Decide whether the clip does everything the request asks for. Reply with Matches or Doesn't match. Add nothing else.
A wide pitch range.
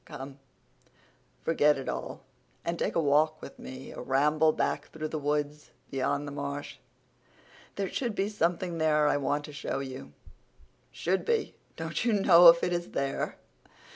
Doesn't match